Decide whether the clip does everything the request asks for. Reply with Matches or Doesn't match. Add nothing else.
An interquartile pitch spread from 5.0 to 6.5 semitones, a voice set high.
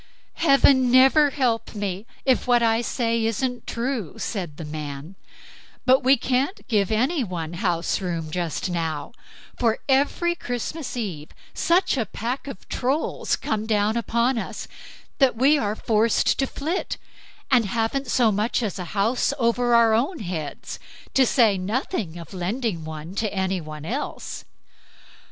Matches